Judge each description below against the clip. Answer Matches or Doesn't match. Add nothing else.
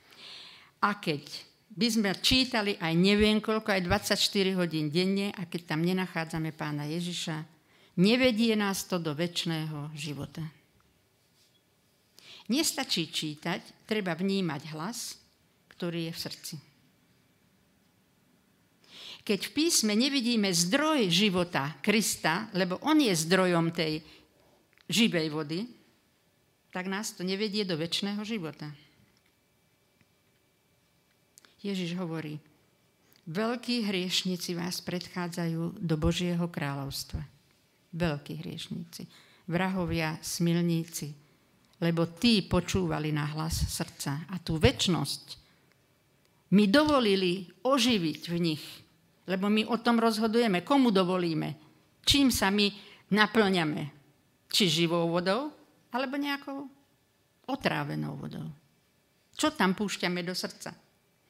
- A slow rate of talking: Matches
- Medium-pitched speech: Matches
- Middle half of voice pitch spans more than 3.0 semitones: Matches